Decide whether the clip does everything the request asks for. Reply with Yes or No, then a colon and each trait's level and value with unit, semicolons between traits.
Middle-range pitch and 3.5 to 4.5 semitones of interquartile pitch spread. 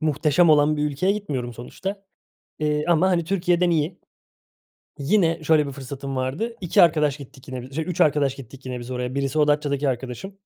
Yes: medium, 150 Hz; average, 4.0 semitones